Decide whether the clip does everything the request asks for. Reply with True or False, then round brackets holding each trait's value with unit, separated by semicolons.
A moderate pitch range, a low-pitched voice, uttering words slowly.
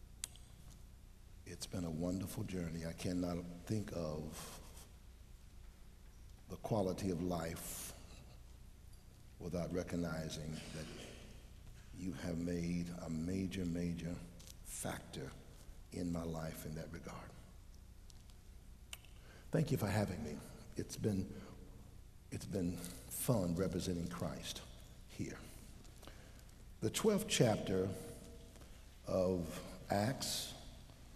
False (2.3 semitones; 90 Hz; 90 wpm)